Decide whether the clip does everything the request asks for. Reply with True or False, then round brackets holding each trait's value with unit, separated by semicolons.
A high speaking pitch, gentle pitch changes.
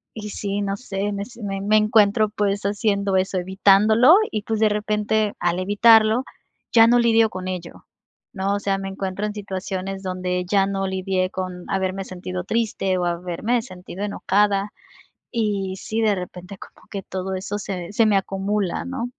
True (200 Hz; 2.1 semitones)